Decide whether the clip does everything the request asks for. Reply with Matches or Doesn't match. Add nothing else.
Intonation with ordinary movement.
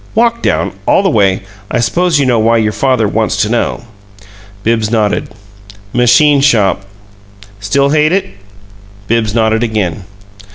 Matches